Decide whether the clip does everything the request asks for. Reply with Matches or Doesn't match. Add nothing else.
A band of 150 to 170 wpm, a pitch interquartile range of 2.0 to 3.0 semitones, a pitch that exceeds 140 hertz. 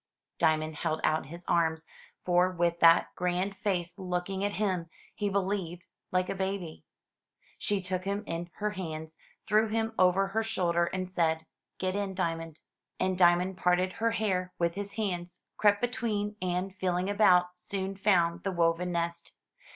Matches